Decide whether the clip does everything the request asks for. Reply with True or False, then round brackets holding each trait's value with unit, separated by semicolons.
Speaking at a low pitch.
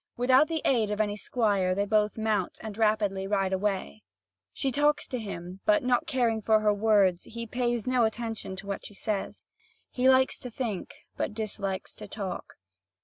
False (215 Hz)